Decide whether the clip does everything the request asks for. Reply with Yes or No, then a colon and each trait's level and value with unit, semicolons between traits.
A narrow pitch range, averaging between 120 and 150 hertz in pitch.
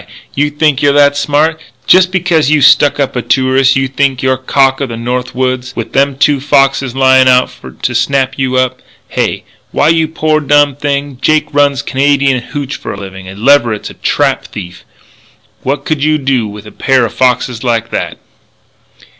Yes: narrow, 2.3 semitones; low, 135 Hz